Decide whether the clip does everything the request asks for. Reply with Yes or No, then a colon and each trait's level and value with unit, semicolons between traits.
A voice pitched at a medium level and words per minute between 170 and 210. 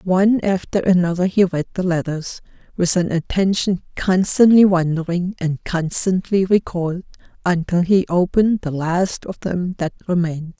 No: medium, 180 Hz; slow, 135 wpm